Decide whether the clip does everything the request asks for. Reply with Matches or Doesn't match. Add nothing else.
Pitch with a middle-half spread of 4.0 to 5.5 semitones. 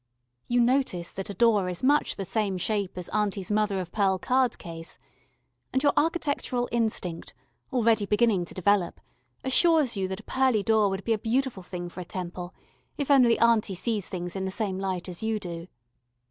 Matches